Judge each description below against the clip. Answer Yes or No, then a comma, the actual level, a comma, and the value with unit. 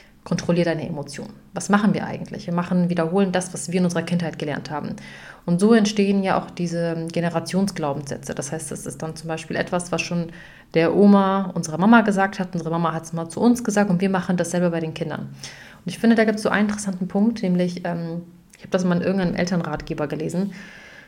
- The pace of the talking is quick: Yes, fast, 215 wpm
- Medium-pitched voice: Yes, medium, 175 Hz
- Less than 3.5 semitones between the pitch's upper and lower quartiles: Yes, average, 2.8 semitones